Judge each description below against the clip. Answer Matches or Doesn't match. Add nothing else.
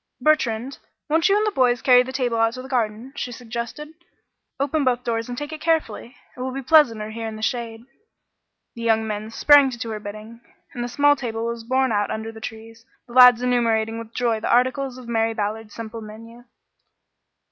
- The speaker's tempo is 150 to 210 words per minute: Matches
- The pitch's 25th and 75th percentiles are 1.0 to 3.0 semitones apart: Matches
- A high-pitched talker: Matches